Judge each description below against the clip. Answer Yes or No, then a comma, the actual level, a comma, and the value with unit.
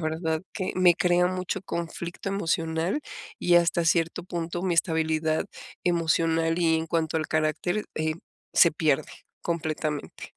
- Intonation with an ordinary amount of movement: No, narrow, 1.6 semitones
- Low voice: No, medium, 165 Hz